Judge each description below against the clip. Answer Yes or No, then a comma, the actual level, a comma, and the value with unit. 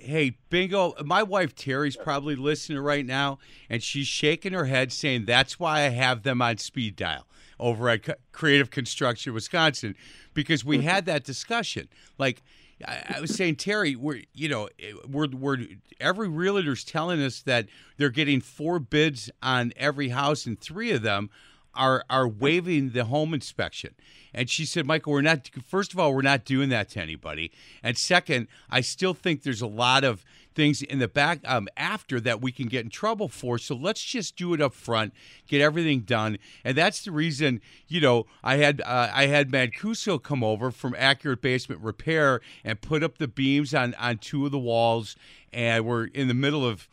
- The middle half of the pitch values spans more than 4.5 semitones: No, average, 3.8 semitones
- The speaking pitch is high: No, medium, 140 Hz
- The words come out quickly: No, average, 190 wpm